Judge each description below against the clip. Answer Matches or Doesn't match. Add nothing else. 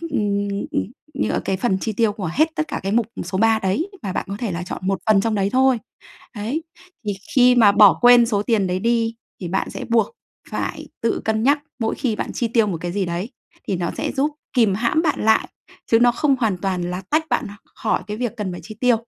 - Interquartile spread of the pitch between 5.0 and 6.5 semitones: Doesn't match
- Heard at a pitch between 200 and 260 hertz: Matches